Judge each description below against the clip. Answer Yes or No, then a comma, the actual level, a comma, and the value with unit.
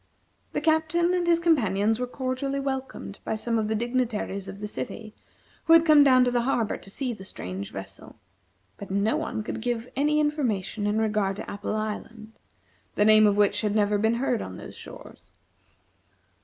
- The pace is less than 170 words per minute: No, average, 185 wpm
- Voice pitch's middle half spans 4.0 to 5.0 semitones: Yes, average, 4.6 semitones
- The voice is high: Yes, high, 225 Hz